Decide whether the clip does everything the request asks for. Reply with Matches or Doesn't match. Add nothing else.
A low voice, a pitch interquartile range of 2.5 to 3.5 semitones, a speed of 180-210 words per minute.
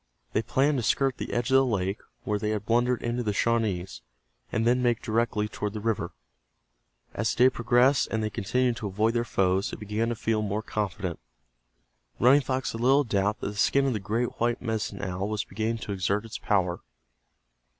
Matches